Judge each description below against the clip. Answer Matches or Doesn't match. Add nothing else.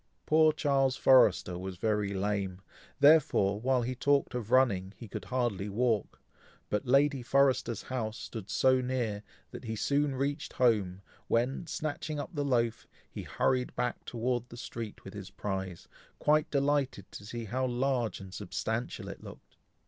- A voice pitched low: Matches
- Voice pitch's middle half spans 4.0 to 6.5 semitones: Matches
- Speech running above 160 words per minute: Doesn't match